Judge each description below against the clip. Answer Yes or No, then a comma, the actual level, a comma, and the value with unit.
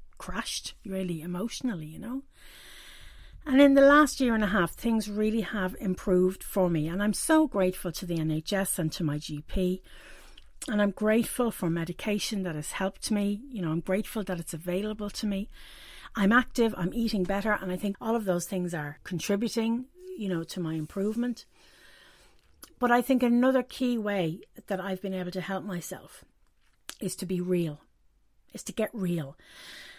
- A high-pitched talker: Yes, high, 195 Hz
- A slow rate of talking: No, average, 175 wpm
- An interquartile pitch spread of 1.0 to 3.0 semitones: No, average, 4.1 semitones